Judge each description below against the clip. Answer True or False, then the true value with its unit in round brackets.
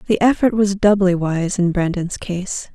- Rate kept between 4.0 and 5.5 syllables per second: True (4.4 syllables/s)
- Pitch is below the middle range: False (190 Hz)